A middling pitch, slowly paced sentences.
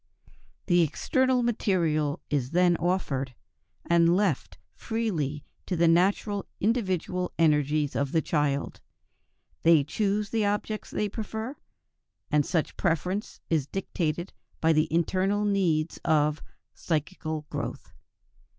Yes: medium, 170 Hz; slow, 115 wpm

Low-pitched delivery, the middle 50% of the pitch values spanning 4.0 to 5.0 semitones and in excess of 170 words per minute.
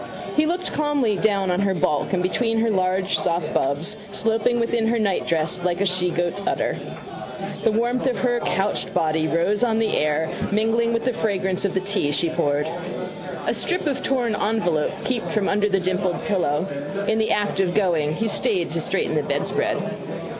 No: high, 200 Hz; average, 4.3 semitones; average, 180 wpm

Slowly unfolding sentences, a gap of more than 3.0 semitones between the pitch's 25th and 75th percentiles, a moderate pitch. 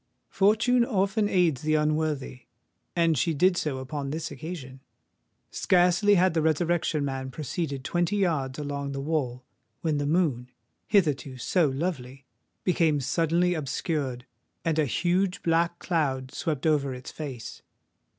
Yes: slow, 130 wpm; average, 4.3 semitones; medium, 155 Hz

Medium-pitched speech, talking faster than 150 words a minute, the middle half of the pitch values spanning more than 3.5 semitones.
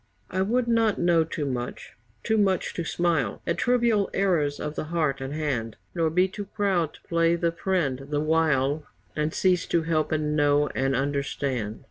Yes: medium, 160 Hz; average, 180 wpm; average, 4.2 semitones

